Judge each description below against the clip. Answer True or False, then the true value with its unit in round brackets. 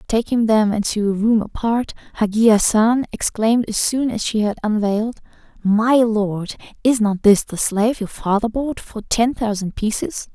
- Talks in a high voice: True (220 Hz)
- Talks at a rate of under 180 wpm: True (170 wpm)